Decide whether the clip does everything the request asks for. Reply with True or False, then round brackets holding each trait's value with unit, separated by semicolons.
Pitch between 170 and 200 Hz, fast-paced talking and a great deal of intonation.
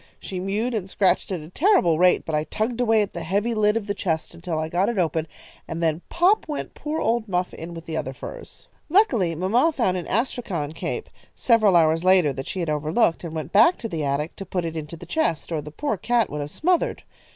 True (185 Hz; 235 wpm; 5.9 semitones)